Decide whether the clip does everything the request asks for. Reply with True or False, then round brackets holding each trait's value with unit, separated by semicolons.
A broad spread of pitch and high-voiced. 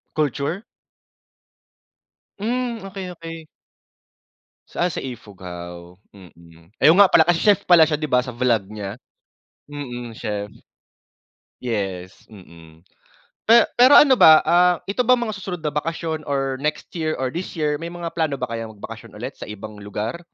False (8.6 semitones; 145 Hz)